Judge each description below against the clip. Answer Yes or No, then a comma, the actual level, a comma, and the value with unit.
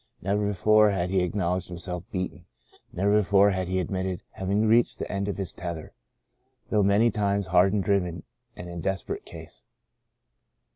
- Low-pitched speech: Yes, very low, 95 Hz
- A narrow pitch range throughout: Yes, narrow, 2.2 semitones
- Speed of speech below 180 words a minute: Yes, average, 160 wpm